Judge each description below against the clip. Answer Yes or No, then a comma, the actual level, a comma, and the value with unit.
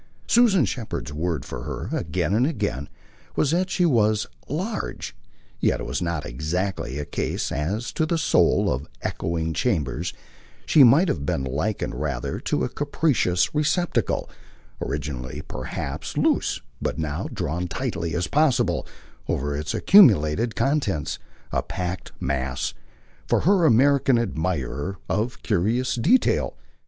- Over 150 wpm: No, slow, 135 wpm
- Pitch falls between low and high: No, very low, 90 Hz